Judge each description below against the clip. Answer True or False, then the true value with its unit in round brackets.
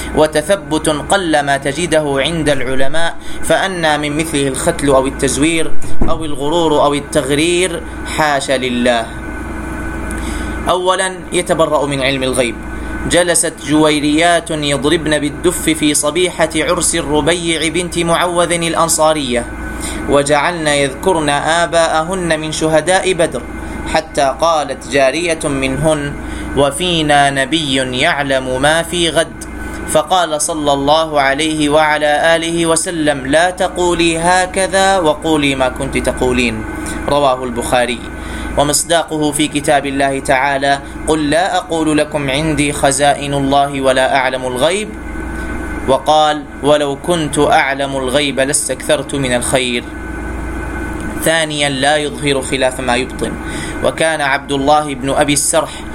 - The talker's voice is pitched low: False (150 Hz)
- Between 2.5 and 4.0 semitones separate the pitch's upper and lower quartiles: True (2.9 semitones)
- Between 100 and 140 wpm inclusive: True (110 wpm)